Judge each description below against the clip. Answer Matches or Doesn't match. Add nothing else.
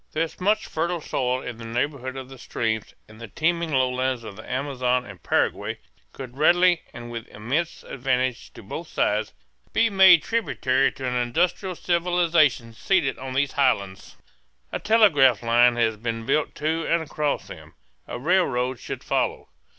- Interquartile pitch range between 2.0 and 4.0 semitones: Doesn't match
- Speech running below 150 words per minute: Doesn't match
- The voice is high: Doesn't match